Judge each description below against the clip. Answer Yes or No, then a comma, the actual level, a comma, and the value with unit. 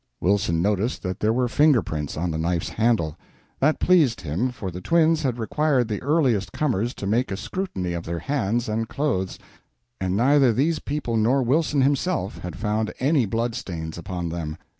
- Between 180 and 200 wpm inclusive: Yes, average, 185 wpm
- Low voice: Yes, low, 115 Hz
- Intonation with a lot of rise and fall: Yes, wide, 6.9 semitones